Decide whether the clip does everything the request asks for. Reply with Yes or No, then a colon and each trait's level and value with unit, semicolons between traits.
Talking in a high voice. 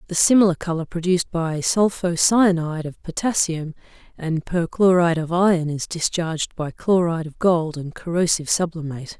No: medium, 170 Hz